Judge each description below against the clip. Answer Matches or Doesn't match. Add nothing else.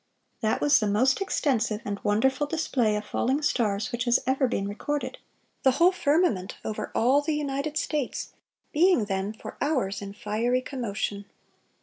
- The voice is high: Matches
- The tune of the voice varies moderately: Doesn't match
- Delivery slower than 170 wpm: Matches